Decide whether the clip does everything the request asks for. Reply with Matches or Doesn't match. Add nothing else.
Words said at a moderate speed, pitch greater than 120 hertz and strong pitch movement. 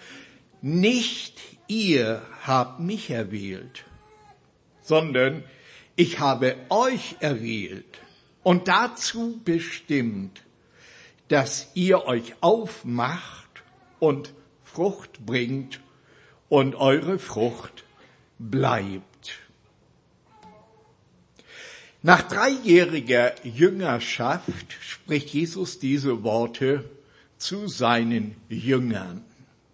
Doesn't match